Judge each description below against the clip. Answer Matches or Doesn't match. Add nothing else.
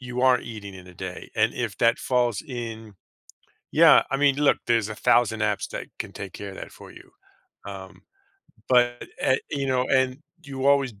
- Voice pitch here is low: Matches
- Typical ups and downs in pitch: Matches